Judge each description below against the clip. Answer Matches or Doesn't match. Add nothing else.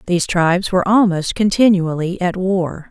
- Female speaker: Matches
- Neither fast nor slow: Matches